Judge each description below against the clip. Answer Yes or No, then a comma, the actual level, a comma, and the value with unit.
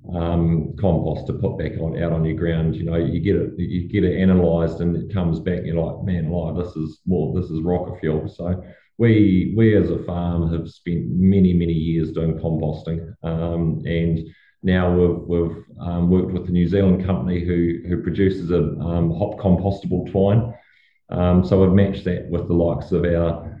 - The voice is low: Yes, very low, 85 Hz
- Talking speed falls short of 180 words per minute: No, average, 200 wpm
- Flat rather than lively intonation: Yes, narrow, 1.7 semitones